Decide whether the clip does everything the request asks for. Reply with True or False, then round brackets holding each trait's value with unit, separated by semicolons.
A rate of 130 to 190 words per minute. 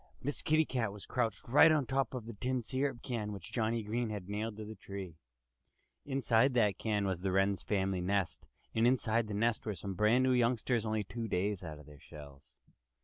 False (205 wpm)